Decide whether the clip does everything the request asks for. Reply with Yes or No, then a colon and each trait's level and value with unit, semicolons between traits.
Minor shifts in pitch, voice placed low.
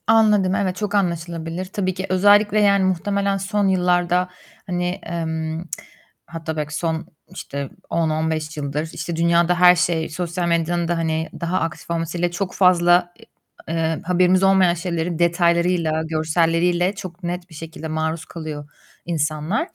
No: narrow, 2.2 semitones; medium, 170 Hz